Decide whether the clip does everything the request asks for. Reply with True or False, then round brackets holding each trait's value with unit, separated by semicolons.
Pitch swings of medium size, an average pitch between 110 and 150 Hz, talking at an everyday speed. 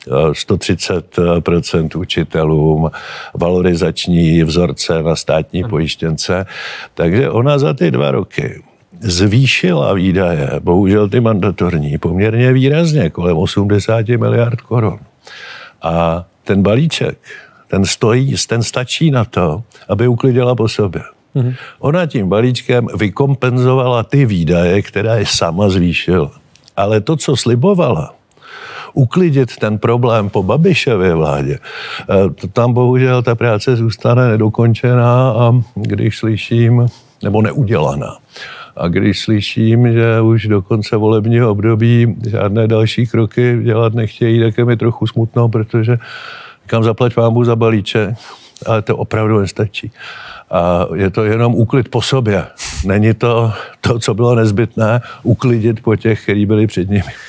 True (3.3 semitones; 115 Hz; 125 wpm)